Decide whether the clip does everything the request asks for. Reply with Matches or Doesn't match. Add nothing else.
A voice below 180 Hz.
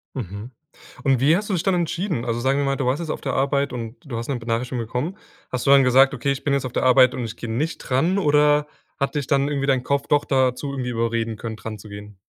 Matches